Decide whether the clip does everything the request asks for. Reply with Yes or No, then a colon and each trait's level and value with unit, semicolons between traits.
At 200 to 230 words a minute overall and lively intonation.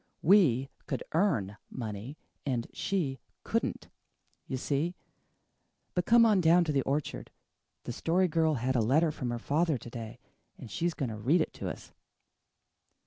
No: average, 160 wpm; wide, 5.8 semitones